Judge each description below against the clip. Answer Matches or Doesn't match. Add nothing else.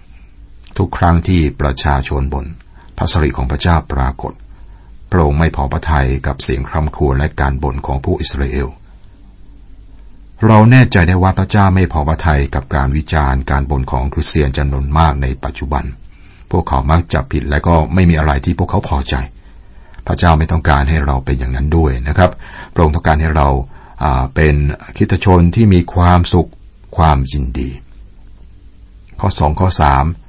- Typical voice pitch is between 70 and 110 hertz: Matches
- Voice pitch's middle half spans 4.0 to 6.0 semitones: Matches